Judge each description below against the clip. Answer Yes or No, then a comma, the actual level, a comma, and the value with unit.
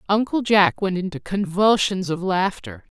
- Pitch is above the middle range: Yes, high, 195 Hz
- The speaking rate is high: No, average, 140 wpm